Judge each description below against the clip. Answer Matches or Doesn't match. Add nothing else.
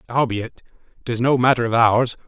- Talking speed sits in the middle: Matches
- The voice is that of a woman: Doesn't match